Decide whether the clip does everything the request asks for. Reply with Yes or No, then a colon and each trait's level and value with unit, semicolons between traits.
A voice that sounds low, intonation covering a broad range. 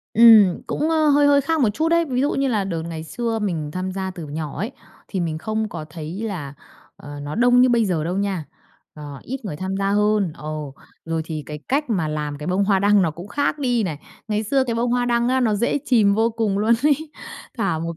No: high, 205 Hz; wide, 6.7 semitones